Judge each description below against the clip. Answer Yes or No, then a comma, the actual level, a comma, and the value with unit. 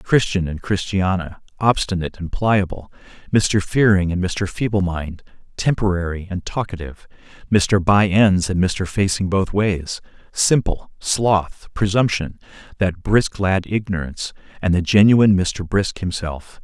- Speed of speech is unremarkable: No, slow, 125 wpm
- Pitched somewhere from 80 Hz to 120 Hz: Yes, very low, 95 Hz